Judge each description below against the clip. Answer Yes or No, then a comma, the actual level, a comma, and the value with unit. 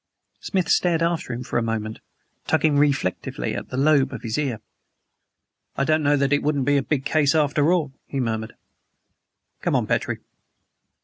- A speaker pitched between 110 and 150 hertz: Yes, medium, 140 Hz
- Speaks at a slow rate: No, average, 175 wpm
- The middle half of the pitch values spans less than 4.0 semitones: Yes, average, 3.3 semitones